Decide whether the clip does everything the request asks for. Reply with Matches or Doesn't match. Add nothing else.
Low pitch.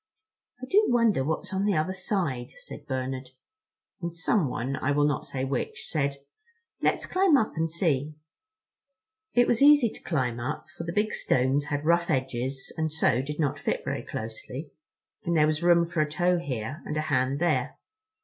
Doesn't match